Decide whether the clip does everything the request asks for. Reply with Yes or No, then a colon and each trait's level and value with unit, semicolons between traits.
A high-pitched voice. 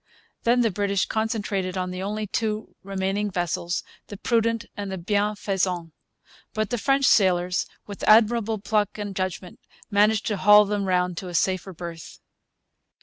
Yes: high, 200 Hz